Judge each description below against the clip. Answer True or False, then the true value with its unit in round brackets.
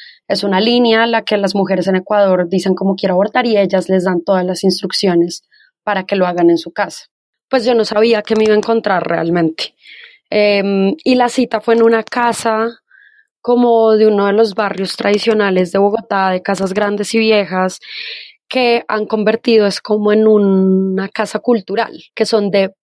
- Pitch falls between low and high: False (210 Hz)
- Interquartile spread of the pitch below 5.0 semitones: True (2.9 semitones)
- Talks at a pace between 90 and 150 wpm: False (190 wpm)